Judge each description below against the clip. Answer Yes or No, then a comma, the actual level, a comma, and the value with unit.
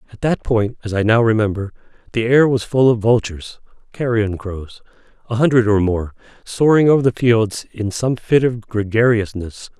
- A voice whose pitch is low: Yes, low, 115 Hz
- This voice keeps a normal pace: Yes, average, 170 wpm